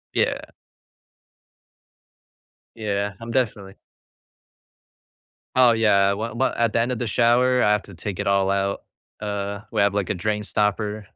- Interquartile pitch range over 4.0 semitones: No, narrow, 2.6 semitones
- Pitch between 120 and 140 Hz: No, low, 105 Hz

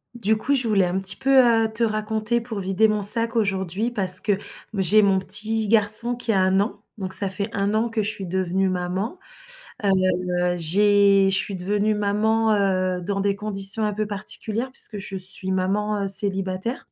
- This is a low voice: No, high, 205 Hz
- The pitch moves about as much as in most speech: No, narrow, 2.2 semitones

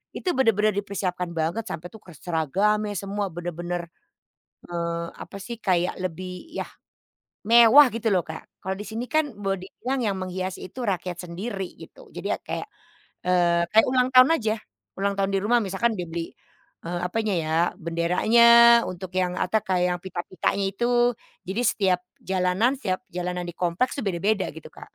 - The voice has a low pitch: No, high, 190 Hz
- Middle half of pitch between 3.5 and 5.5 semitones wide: Yes, average, 3.9 semitones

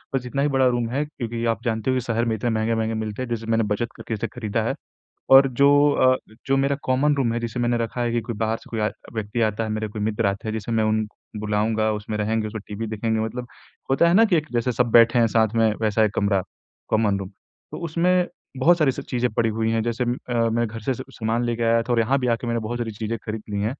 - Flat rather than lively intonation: Yes, narrow, 2.2 semitones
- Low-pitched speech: Yes, low, 115 Hz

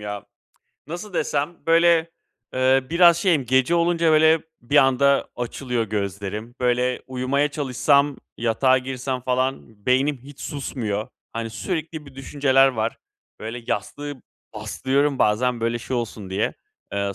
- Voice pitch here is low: Yes, low, 130 Hz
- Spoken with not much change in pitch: No, average, 3.9 semitones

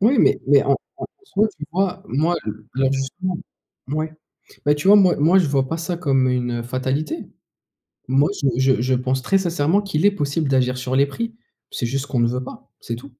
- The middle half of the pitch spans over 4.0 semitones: Yes, average, 5.1 semitones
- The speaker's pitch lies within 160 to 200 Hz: No, medium, 140 Hz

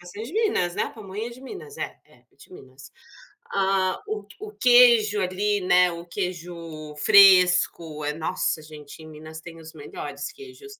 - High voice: No, medium, 180 Hz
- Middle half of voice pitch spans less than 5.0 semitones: No, wide, 5.4 semitones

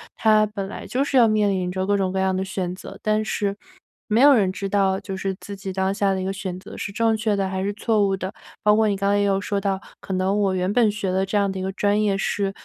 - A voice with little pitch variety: Yes, narrow, 1.7 semitones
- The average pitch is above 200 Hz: No, high, 195 Hz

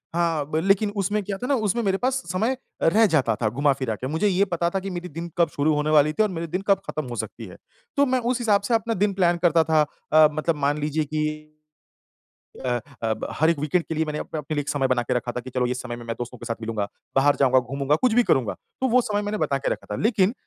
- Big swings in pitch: Yes, wide, 6.3 semitones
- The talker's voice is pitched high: No, medium, 160 Hz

